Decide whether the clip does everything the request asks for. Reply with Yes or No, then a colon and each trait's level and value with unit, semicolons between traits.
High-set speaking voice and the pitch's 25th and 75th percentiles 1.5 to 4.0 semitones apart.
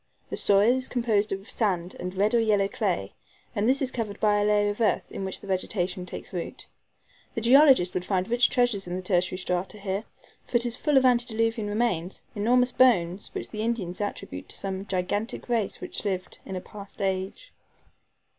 Yes: high, 205 Hz; average, 3.7 semitones